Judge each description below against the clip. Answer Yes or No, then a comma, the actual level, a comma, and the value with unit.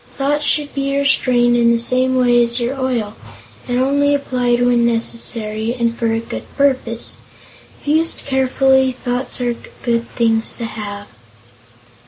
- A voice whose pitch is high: Yes, high, 245 Hz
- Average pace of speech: Yes, average, 150 wpm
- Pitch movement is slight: Yes, narrow, 2.3 semitones